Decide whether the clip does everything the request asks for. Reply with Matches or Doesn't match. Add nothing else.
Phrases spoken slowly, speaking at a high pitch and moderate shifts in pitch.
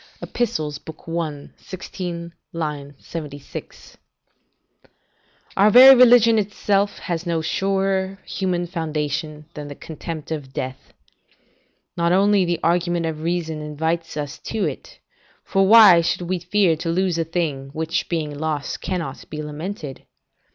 Doesn't match